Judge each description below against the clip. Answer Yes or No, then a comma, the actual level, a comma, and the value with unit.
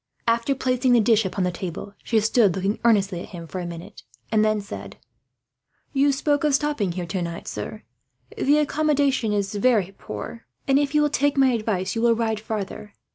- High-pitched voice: Yes, high, 220 Hz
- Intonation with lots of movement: Yes, wide, 5.7 semitones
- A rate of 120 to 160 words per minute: No, average, 190 wpm